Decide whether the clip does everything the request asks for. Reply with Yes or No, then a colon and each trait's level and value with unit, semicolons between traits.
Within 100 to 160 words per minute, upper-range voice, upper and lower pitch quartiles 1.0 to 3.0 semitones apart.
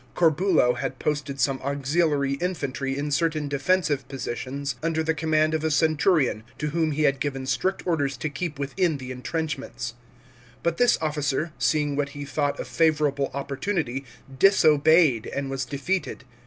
No: average, 155 wpm; medium, 145 Hz; average, 2.7 semitones